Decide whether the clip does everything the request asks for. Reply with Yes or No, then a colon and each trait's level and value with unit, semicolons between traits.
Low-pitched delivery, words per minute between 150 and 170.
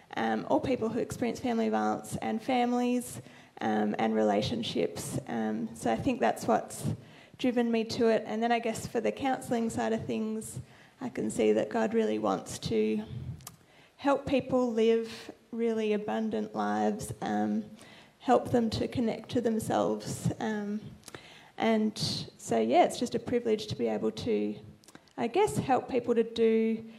No: high, 220 Hz; average, 160 wpm